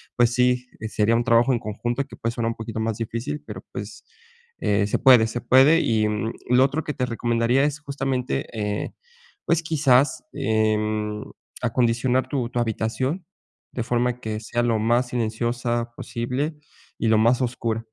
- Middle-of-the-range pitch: No, low, 120 Hz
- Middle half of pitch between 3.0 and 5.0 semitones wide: No, narrow, 2.5 semitones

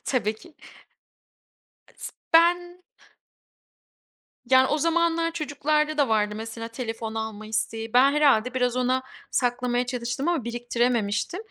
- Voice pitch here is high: Yes, very high, 250 Hz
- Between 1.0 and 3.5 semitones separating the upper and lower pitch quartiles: No, average, 5.0 semitones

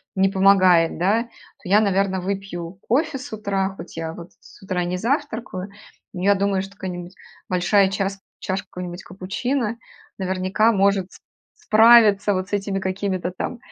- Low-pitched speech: No, high, 195 Hz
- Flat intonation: Yes, narrow, 2.0 semitones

